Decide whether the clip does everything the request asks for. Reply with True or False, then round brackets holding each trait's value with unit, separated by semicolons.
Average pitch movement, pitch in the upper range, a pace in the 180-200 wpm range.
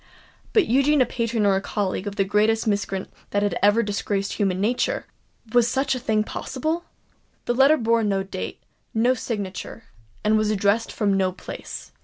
False (3.4 semitones; 215 Hz; 160 wpm)